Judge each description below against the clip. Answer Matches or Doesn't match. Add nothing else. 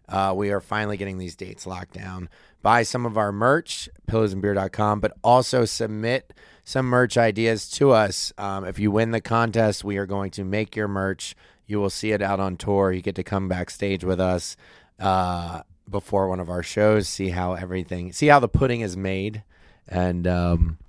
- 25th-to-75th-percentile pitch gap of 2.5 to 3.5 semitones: Matches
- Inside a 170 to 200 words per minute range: Matches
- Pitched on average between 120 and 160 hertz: Doesn't match